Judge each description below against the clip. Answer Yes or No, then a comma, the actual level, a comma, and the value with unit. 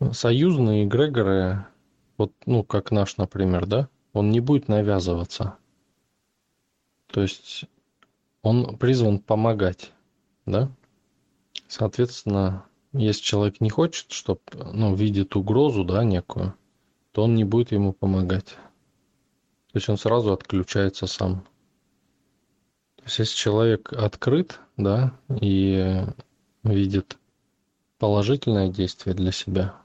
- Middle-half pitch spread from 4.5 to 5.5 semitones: No, average, 3.8 semitones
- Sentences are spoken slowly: Yes, slow, 105 wpm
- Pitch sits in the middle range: No, low, 105 Hz